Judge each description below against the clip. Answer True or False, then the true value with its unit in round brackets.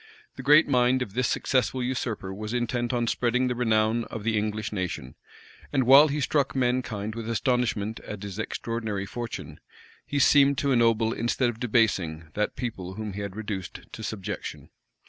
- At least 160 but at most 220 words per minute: True (170 wpm)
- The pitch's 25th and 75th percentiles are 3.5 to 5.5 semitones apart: False (3.0 semitones)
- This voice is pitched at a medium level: False (115 Hz)